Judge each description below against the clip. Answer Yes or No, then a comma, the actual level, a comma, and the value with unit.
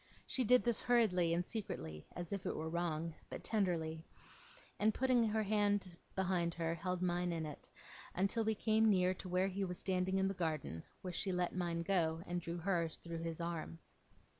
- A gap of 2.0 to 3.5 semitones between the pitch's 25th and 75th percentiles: Yes, average, 2.9 semitones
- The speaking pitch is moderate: Yes, medium, 180 Hz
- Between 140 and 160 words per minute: No, average, 195 wpm